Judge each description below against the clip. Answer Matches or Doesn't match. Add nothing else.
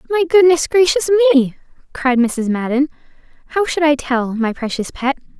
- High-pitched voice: Matches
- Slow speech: Doesn't match